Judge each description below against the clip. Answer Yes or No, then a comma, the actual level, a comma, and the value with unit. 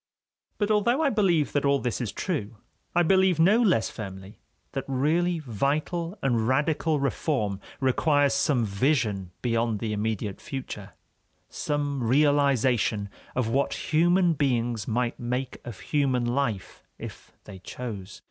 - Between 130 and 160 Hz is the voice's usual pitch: Yes, low, 135 Hz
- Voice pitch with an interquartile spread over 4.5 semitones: Yes, wide, 5.4 semitones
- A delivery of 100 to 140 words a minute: Yes, slow, 135 wpm